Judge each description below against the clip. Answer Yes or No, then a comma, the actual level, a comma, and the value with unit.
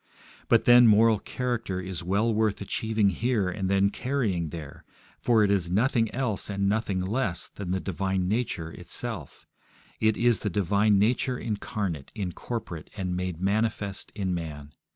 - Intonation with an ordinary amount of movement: Yes, average, 3.4 semitones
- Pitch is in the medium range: No, low, 100 Hz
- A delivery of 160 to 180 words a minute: No, average, 150 wpm